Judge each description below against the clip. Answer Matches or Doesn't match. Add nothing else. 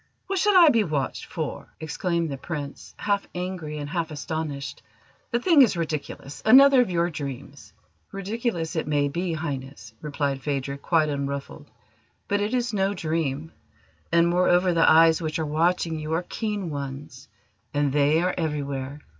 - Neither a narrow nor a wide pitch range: Matches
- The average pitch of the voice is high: Doesn't match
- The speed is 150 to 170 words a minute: Matches